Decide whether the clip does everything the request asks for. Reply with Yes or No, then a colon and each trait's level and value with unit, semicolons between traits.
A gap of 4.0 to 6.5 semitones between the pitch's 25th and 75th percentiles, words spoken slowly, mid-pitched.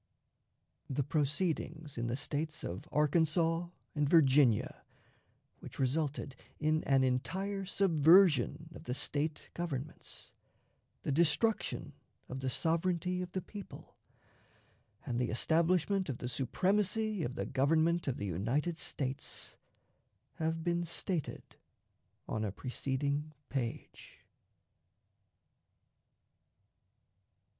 Yes: average, 4.4 semitones; slow, 100 wpm; medium, 155 Hz